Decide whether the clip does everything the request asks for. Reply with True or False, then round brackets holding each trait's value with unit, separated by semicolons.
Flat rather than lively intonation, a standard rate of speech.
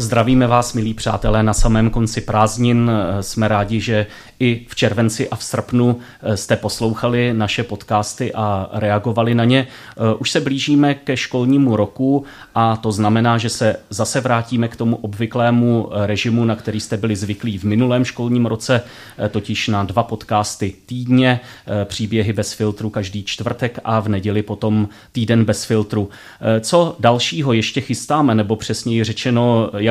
True (2.2 semitones; 155 wpm)